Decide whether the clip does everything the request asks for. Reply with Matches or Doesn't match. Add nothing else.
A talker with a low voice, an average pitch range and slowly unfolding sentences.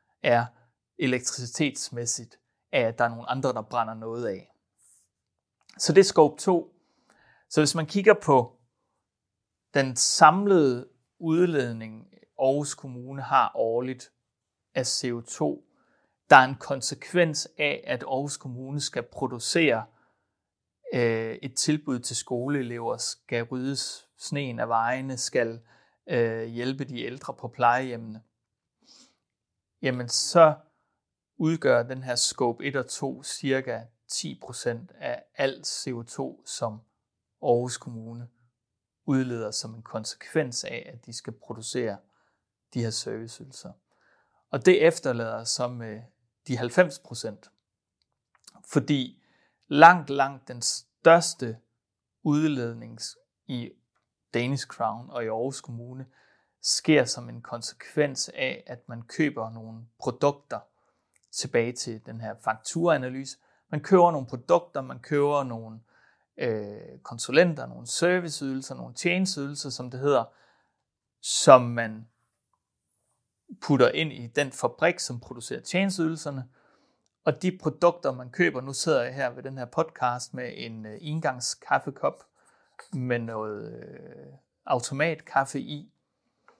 Matches